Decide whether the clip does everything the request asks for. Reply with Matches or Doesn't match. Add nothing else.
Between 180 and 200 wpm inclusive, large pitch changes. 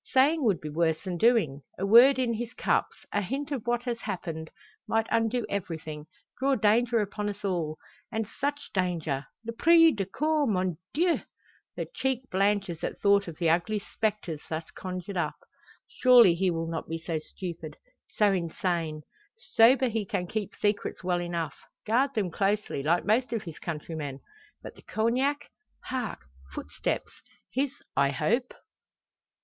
Doesn't match